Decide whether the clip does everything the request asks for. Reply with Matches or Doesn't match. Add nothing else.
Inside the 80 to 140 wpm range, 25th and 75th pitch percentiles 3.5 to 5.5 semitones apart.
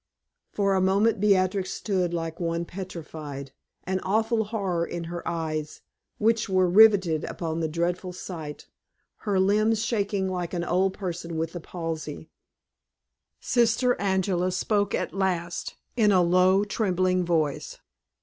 Doesn't match